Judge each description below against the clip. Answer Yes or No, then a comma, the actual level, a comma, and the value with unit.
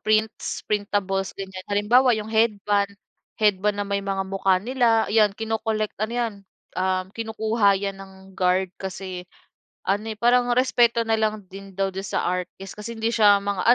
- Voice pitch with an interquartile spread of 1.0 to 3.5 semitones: Yes, narrow, 2.4 semitones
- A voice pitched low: No, high, 205 Hz